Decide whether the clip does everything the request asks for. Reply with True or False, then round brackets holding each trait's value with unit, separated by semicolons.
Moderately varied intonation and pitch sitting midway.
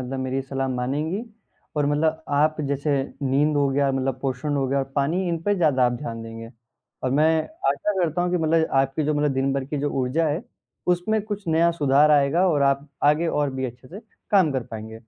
True (3.2 semitones; 145 Hz)